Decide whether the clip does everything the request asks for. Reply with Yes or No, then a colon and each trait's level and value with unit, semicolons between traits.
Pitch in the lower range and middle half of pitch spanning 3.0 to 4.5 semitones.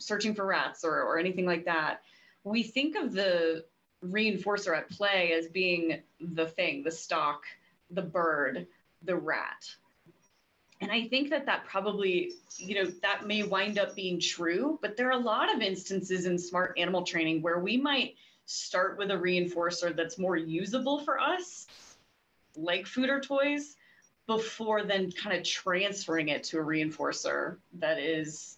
No: medium, 185 Hz; average, 3.7 semitones